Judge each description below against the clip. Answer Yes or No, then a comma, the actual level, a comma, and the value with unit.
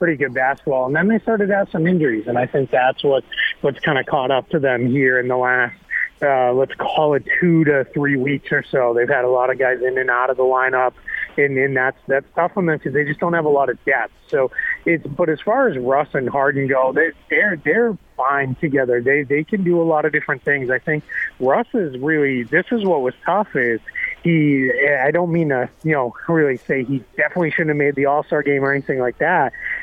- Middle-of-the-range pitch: Yes, medium, 145 Hz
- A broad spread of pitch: No, average, 4.3 semitones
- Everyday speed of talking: No, fast, 245 wpm